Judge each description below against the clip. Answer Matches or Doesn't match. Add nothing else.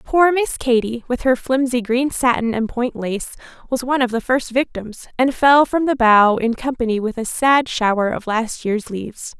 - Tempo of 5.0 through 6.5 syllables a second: Doesn't match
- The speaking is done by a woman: Matches